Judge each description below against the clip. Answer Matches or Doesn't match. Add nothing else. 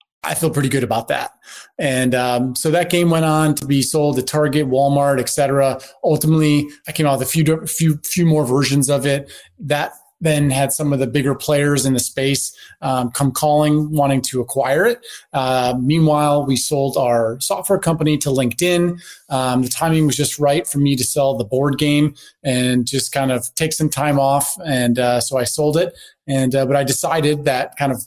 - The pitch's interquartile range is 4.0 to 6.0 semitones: Doesn't match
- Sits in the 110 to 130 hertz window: Doesn't match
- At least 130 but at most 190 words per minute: Doesn't match